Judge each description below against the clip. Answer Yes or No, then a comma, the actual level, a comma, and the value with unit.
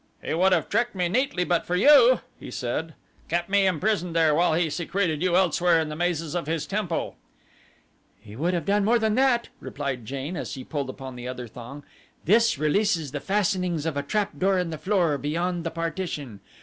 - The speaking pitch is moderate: Yes, medium, 170 Hz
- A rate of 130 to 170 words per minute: No, average, 200 wpm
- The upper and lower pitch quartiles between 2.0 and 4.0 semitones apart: No, average, 4.5 semitones